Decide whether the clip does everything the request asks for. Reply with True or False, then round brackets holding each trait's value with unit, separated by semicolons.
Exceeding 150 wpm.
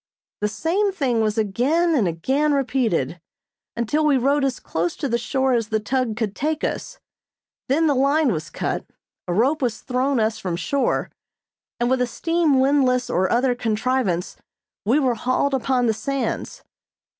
True (165 wpm)